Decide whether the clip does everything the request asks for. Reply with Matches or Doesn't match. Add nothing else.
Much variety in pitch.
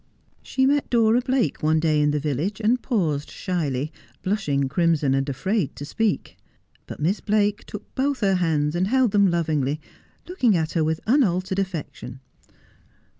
Matches